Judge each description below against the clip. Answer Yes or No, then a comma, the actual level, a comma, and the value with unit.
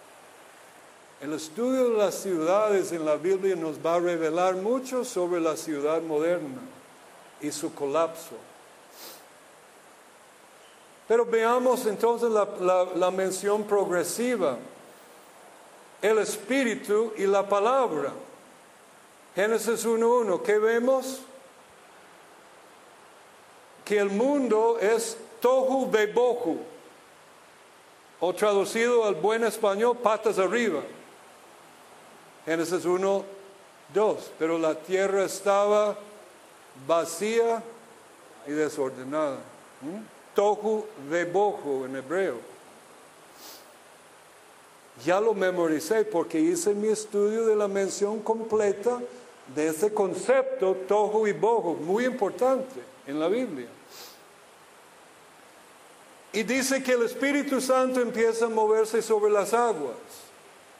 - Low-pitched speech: No, high, 210 Hz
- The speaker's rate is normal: No, slow, 100 wpm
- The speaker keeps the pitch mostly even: No, average, 4.4 semitones